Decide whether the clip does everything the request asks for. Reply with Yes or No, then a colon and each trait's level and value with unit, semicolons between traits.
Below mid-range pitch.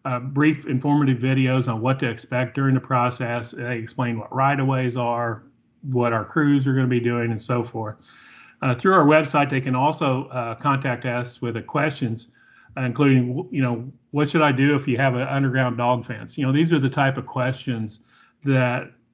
Yes: low, 130 Hz